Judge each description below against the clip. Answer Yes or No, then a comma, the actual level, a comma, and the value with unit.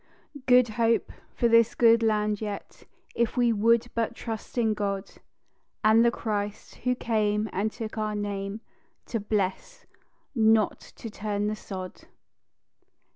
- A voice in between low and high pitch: No, high, 215 Hz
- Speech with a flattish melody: Yes, narrow, 1.9 semitones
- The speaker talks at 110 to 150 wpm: Yes, slow, 135 wpm